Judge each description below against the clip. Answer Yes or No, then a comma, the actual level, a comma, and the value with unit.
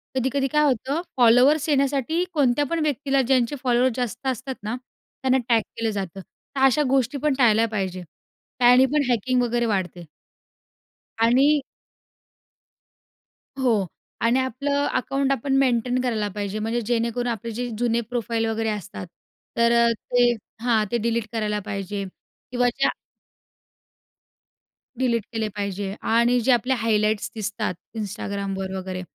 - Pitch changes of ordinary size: Yes, average, 3.4 semitones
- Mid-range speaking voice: No, high, 235 Hz